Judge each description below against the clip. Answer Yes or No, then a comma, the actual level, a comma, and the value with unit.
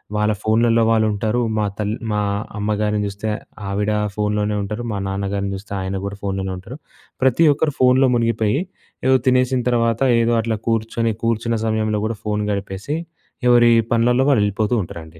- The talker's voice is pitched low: Yes, low, 110 Hz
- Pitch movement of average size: No, narrow, 2.3 semitones